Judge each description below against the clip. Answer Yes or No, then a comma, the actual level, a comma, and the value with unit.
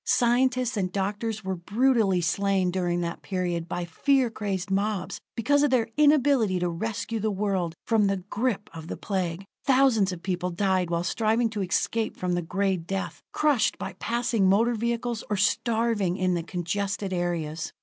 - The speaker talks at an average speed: Yes, average, 170 wpm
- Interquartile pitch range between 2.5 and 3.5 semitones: No, average, 4.2 semitones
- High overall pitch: Yes, high, 200 Hz